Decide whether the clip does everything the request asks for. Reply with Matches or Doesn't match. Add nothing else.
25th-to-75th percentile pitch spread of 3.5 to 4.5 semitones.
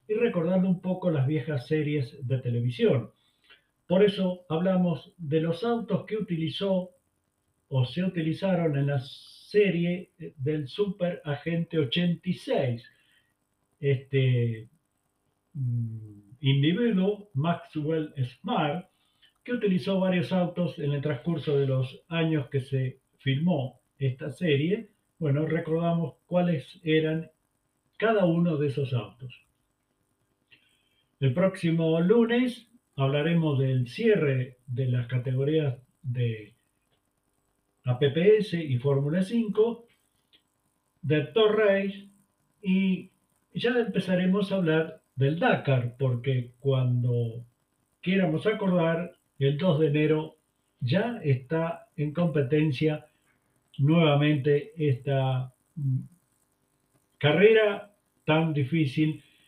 Doesn't match